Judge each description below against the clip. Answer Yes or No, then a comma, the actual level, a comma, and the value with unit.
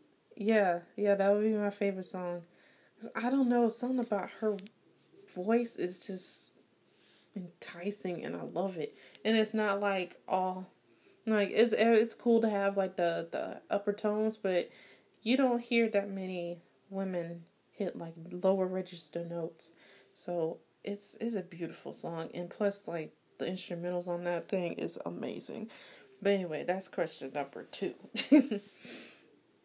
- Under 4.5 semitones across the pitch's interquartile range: Yes, average, 3.7 semitones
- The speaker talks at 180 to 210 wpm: No, average, 145 wpm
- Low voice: No, high, 195 Hz